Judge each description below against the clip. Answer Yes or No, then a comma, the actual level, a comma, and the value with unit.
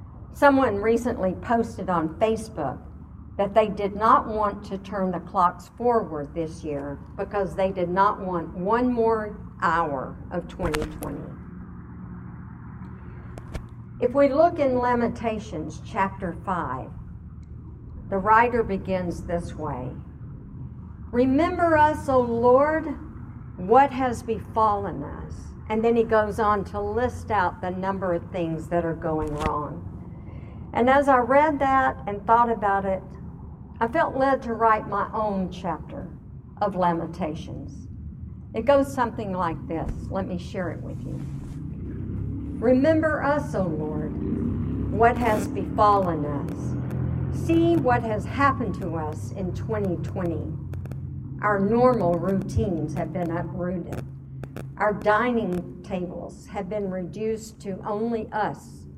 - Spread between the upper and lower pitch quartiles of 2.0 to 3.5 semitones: No, average, 5.2 semitones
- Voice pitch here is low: No, high, 205 Hz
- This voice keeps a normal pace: No, slow, 125 wpm